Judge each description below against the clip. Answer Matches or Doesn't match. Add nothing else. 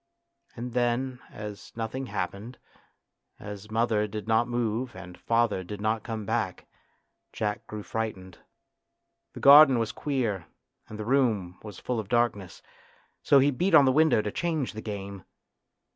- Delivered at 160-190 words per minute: Doesn't match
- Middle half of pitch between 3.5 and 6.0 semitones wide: Doesn't match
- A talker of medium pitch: Doesn't match